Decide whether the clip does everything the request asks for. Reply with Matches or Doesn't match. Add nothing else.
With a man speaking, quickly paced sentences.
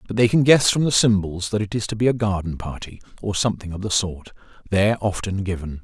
Matches